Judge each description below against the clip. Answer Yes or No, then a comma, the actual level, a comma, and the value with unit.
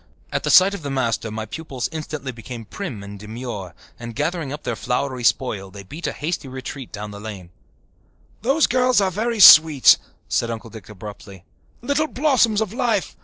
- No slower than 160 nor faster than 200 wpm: Yes, average, 180 wpm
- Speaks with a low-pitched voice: Yes, low, 130 Hz